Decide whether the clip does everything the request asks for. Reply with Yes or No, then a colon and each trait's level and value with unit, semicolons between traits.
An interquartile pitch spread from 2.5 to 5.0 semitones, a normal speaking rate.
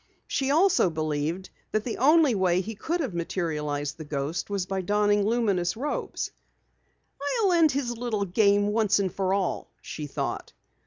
No: wide, 5.6 semitones; average, 160 wpm